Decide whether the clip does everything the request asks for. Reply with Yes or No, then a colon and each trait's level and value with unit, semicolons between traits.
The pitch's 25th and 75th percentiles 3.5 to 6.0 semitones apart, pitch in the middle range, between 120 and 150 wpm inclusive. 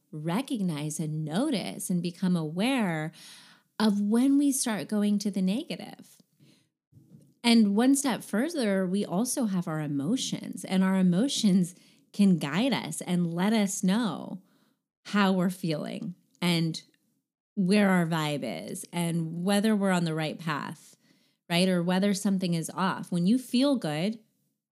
No: average, 4.0 semitones; high, 195 Hz; average, 140 wpm